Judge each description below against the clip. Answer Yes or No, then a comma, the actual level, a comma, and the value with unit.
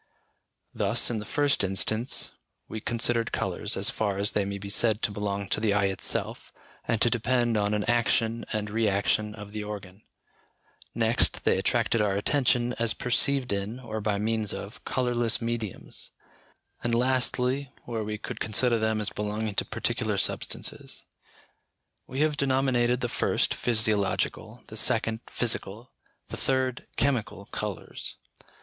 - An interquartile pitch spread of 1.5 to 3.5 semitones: Yes, average, 2.7 semitones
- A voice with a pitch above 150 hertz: No, low, 110 Hz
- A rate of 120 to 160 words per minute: Yes, average, 150 wpm